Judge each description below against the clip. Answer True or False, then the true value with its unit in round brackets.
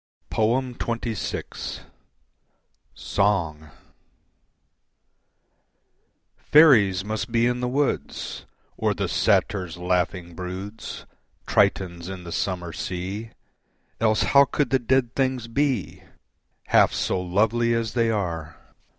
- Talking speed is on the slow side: True (100 wpm)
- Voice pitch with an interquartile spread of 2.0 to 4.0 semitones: False (4.8 semitones)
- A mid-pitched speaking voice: False (105 Hz)